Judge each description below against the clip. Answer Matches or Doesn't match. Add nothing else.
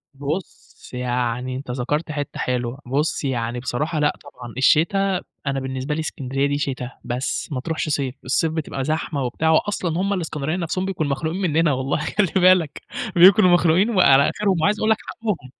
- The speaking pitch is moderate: Matches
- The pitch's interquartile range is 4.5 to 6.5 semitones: Matches